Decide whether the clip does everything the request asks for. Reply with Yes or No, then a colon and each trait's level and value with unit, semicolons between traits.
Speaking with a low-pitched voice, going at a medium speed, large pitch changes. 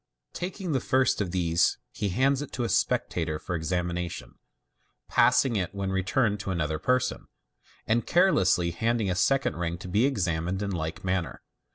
Yes: very low, 95 Hz; average, 170 wpm; wide, 6.4 semitones